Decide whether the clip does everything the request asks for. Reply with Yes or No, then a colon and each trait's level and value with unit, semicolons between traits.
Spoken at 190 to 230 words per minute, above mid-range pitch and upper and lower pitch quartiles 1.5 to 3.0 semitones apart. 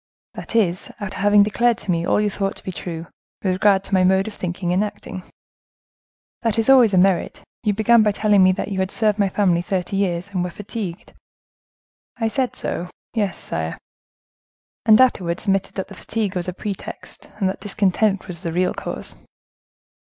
Yes: average, 195 wpm; high, 195 Hz; narrow, 2.6 semitones